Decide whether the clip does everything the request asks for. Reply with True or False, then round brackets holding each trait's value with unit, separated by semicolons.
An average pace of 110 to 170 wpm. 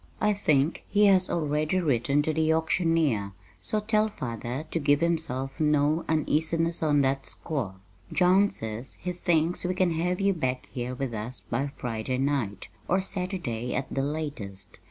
True (160 wpm)